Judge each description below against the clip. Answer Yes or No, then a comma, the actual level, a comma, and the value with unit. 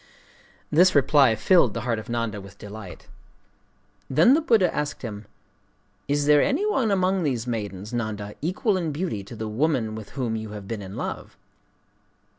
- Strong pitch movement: Yes, wide, 7.2 semitones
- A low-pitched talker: Yes, low, 120 Hz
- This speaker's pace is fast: No, average, 170 wpm